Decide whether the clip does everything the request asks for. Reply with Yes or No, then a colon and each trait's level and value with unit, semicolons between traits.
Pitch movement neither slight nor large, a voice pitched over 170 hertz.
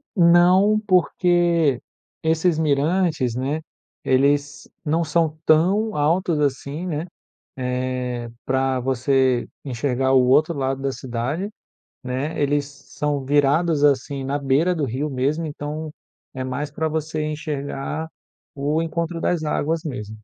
No: average, 3.4 semitones; medium, 145 Hz